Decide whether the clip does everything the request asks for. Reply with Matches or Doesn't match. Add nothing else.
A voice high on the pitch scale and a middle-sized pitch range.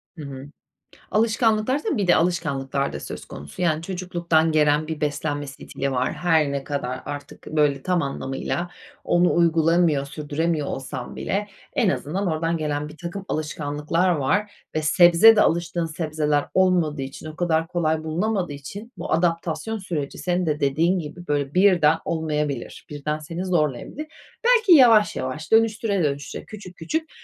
Doesn't match